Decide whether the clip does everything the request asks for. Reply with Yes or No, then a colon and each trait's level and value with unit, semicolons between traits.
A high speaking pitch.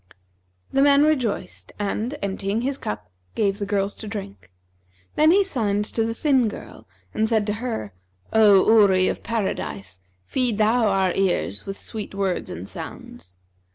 Yes: high, 210 Hz